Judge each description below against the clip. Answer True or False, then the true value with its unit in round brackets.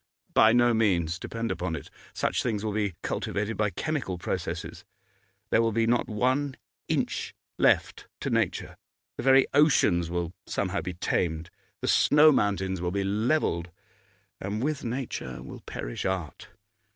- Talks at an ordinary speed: True (150 wpm)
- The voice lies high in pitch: False (105 Hz)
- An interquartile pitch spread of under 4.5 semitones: False (5.2 semitones)